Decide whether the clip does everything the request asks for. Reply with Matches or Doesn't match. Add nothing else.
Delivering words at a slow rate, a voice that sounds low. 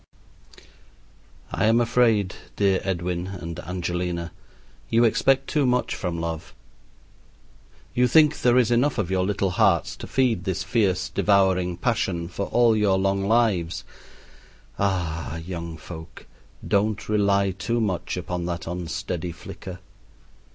Matches